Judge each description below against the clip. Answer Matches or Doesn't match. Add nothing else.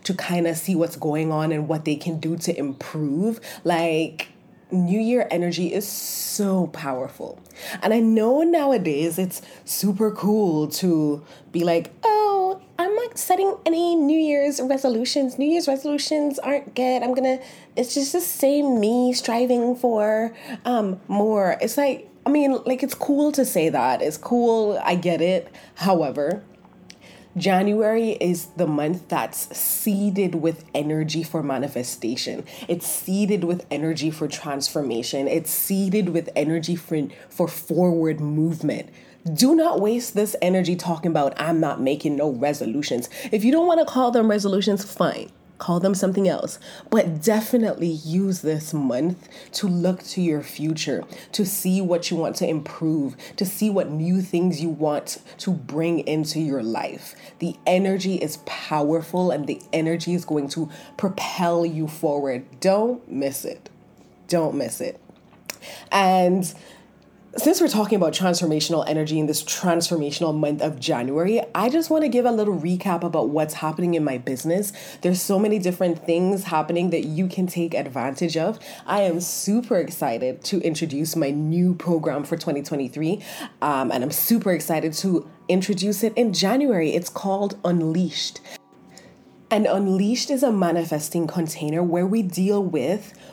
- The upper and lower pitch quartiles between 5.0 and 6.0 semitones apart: Matches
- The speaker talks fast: Doesn't match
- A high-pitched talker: Doesn't match